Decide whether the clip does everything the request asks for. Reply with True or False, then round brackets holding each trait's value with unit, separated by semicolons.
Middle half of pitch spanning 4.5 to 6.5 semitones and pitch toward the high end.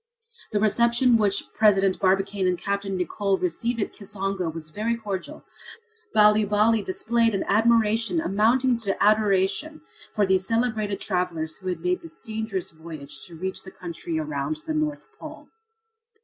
False (3.4 semitones; 205 Hz)